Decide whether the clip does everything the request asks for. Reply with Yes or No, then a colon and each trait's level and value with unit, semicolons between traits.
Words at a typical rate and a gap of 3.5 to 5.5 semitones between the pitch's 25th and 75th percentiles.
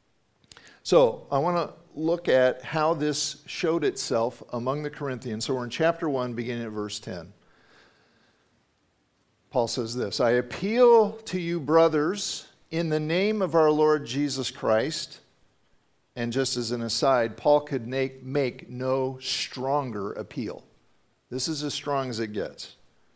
Yes: average, 150 wpm; average, 4.4 semitones